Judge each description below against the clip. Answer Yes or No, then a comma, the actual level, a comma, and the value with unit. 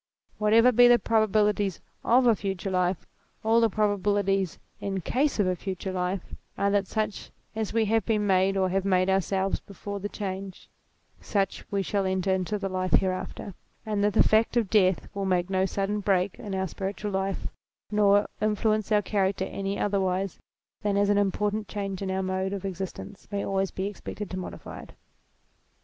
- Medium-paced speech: Yes, average, 180 wpm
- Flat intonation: Yes, narrow, 1.7 semitones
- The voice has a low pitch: No, high, 195 Hz